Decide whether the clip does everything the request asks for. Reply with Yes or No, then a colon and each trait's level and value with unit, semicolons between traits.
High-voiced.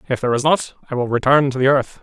No: low, 135 Hz